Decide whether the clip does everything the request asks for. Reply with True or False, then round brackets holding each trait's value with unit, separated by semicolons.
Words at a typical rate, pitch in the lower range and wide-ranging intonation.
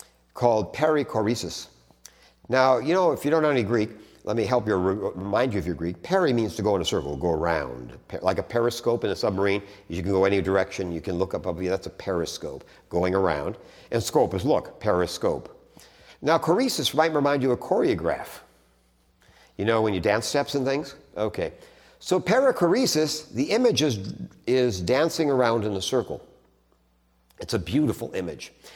True (180 wpm; 115 Hz; 7.7 semitones)